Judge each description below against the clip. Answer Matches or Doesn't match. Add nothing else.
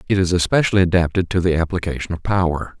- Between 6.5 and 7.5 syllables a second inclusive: Matches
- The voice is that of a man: Matches